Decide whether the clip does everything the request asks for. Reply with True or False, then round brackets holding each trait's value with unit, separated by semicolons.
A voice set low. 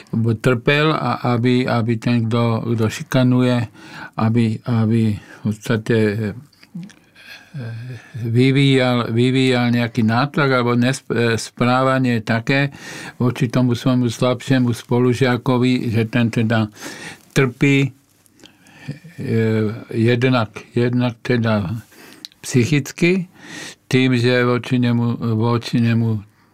True (125 Hz)